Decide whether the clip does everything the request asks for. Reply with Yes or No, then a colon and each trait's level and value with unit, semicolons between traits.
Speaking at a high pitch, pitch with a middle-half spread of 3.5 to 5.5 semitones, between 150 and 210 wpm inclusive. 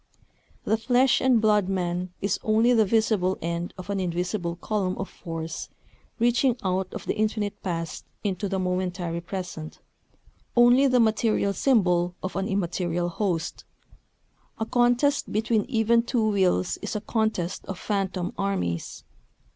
No: high, 195 Hz; average, 3.8 semitones; average, 140 wpm